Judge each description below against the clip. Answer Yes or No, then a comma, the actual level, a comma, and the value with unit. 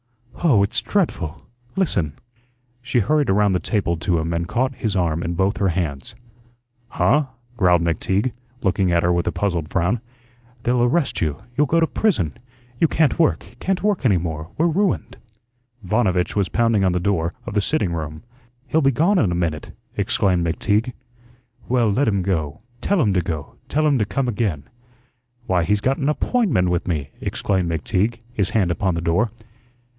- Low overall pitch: Yes, low, 100 Hz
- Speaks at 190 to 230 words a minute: No, average, 180 wpm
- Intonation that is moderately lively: No, wide, 6.7 semitones